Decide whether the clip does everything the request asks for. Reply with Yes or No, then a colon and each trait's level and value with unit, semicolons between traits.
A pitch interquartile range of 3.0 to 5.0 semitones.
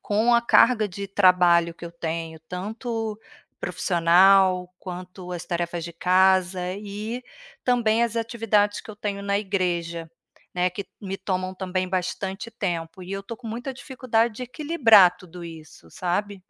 Yes: average, 3.4 semitones